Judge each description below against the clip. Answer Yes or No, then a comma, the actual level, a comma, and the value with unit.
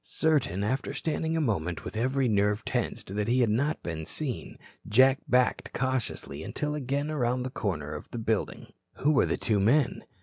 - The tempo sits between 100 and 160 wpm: No, average, 180 wpm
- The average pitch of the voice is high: No, low, 125 Hz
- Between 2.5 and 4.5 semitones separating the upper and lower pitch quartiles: No, average, 5.1 semitones